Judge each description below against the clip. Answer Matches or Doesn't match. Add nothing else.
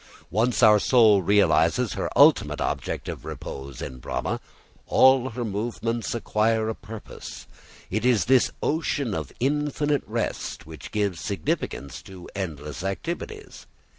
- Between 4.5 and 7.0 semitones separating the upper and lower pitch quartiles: Matches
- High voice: Doesn't match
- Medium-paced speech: Doesn't match